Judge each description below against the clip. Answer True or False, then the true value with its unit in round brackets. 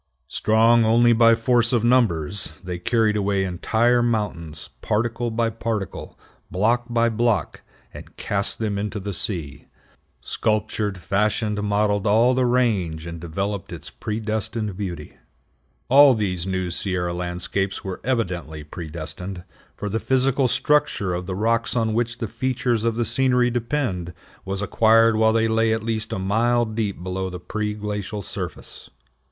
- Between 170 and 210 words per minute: False (145 wpm)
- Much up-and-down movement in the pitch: False (3.6 semitones)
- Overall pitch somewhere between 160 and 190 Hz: False (110 Hz)